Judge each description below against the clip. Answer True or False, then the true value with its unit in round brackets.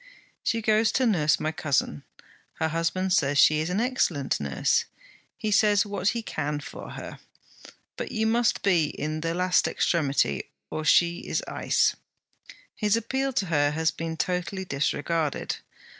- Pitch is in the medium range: True (170 Hz)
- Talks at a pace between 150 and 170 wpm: True (155 wpm)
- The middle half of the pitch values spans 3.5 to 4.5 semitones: False (5.4 semitones)